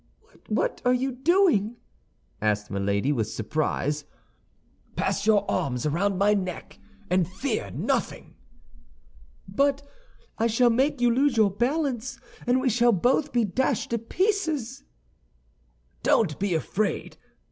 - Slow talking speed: Yes, slow, 125 wpm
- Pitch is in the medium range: No, high, 225 Hz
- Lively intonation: Yes, wide, 6.3 semitones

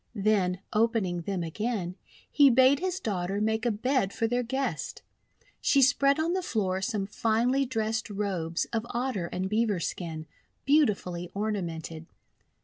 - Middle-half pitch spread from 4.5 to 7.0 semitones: Yes, average, 5.1 semitones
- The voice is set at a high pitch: Yes, high, 215 Hz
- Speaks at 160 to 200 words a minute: No, average, 140 wpm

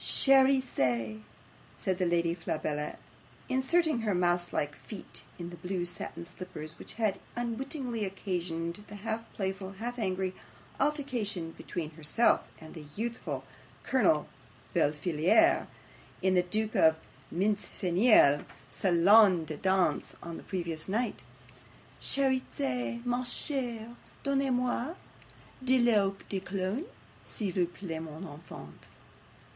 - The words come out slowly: Yes, slow, 120 wpm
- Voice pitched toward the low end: No, high, 190 Hz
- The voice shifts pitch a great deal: Yes, wide, 5.9 semitones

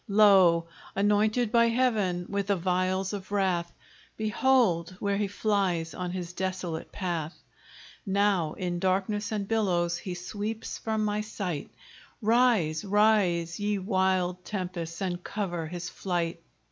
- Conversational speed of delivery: No, slow, 130 wpm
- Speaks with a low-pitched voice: No, high, 190 Hz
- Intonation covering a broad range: No, average, 3.0 semitones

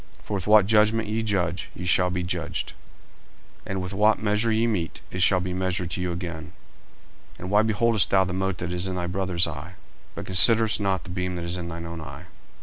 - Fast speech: Yes, fast, 230 wpm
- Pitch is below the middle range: Yes, very low, 95 Hz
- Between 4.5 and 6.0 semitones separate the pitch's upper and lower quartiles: No, average, 2.9 semitones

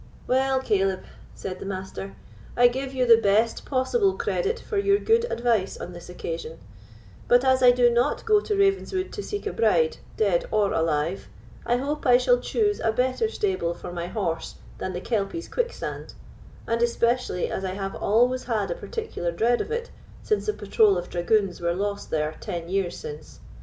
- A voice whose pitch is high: Yes, high, 235 Hz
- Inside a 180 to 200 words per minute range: Yes, average, 185 wpm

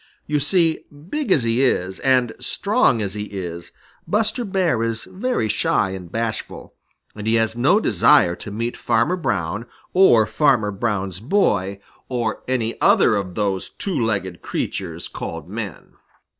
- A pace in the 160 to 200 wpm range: No, average, 150 wpm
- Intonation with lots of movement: Yes, wide, 6.1 semitones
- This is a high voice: No, low, 115 Hz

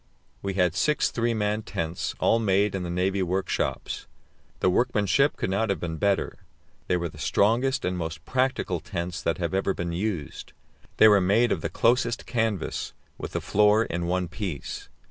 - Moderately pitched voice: No, very low, 95 Hz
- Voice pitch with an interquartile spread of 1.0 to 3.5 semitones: No, average, 3.9 semitones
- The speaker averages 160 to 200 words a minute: Yes, average, 180 wpm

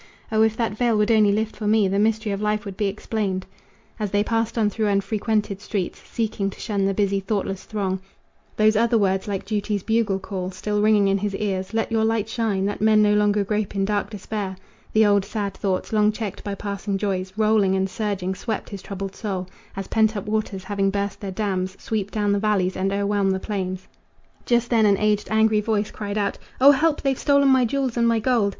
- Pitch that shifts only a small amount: Yes, narrow, 1.9 semitones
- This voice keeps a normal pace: No, fast, 215 wpm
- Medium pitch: No, high, 210 Hz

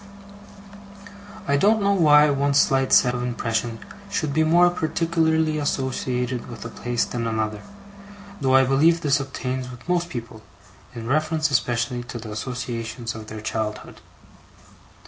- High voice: No, low, 130 Hz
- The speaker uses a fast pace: No, average, 145 wpm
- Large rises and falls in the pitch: No, average, 4.8 semitones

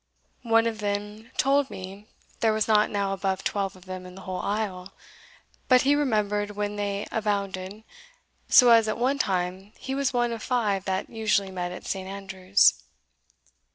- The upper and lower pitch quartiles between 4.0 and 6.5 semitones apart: No, average, 2.8 semitones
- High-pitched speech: Yes, high, 205 Hz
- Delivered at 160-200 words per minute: Yes, average, 170 wpm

